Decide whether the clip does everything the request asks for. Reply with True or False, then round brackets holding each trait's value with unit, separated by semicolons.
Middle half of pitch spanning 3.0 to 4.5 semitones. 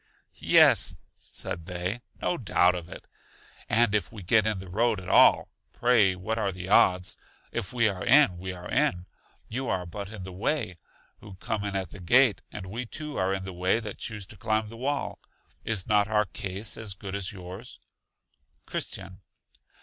True (3.4 semitones)